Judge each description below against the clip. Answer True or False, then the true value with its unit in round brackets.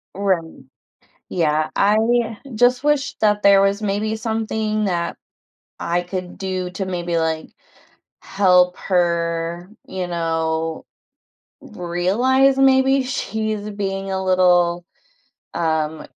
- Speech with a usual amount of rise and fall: True (4.0 semitones)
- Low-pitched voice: False (190 Hz)